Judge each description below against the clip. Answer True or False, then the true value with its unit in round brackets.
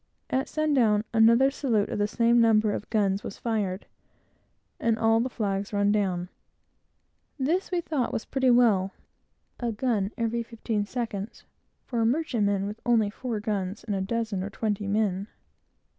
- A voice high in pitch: True (220 Hz)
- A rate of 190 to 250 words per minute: False (160 wpm)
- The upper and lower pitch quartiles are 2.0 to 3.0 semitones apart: True (2.7 semitones)